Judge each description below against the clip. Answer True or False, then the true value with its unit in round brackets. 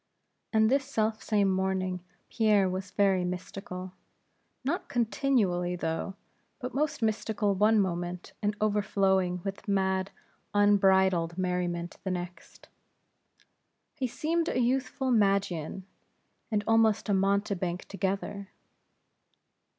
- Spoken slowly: True (105 wpm)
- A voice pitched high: True (195 Hz)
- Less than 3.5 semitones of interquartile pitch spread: True (2.9 semitones)